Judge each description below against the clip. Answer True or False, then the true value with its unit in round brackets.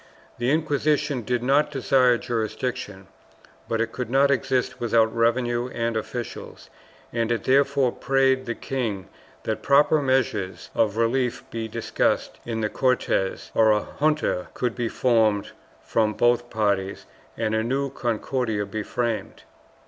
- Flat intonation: False (3.0 semitones)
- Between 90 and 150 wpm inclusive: True (140 wpm)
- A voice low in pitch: True (120 Hz)